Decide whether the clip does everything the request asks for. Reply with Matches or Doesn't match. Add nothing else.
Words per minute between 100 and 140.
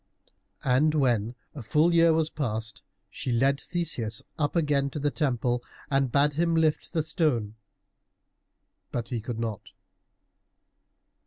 Matches